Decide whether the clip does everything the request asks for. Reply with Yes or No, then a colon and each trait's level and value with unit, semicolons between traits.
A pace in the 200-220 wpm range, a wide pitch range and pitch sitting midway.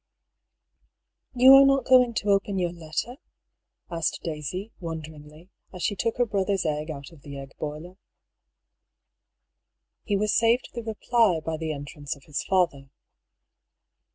No: average, 140 wpm; wide, 6.0 semitones; medium, 175 Hz